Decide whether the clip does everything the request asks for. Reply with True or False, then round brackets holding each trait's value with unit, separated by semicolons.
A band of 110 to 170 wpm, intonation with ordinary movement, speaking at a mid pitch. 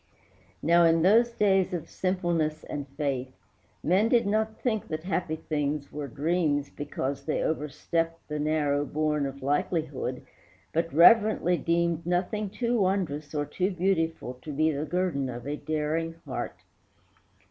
True (145 wpm; 3.7 semitones; 160 Hz)